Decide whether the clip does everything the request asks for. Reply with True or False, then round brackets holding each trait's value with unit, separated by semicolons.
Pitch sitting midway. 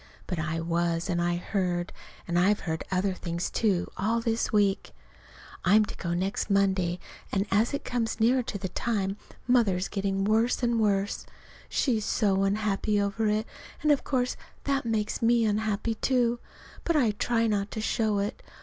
False (205 Hz)